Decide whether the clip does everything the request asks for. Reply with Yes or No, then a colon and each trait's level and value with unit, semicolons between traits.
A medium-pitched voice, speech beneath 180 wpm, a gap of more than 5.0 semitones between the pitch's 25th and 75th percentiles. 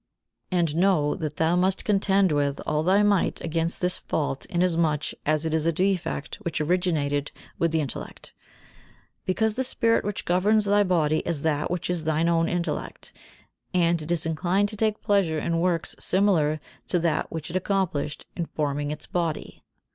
No: medium, 170 Hz; average, 170 wpm; average, 3.3 semitones